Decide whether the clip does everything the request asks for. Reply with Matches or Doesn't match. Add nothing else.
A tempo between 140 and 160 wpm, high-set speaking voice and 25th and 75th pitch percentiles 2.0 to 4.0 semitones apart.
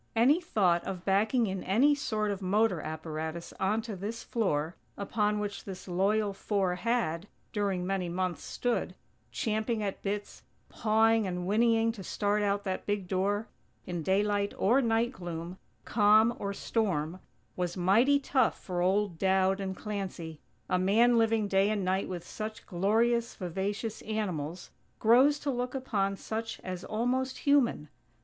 Matches